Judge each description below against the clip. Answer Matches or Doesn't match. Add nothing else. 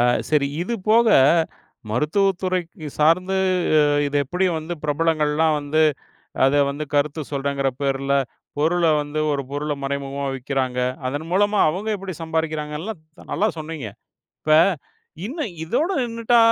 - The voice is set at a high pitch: Doesn't match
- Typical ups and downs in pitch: Matches